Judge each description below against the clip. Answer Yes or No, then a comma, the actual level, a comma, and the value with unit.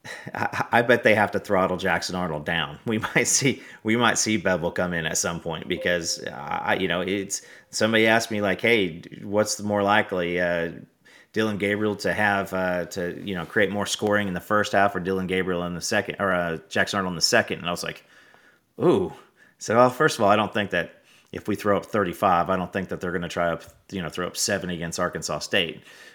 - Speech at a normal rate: No, fast, 230 wpm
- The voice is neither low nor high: No, very low, 95 Hz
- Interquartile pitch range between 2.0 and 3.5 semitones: Yes, average, 2.7 semitones